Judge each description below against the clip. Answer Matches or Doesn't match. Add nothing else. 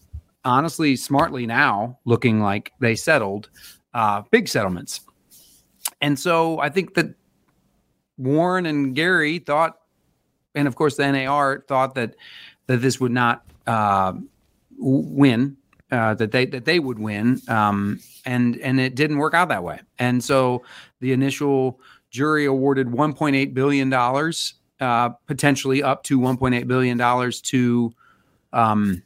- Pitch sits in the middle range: Doesn't match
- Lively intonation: Doesn't match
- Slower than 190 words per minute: Matches